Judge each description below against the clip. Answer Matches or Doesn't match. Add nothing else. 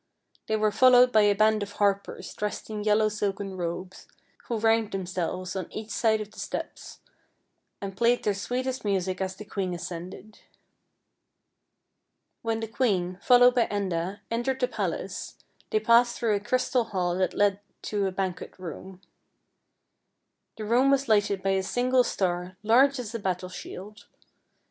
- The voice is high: Matches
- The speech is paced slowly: Doesn't match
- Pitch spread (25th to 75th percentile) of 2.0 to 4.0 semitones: Matches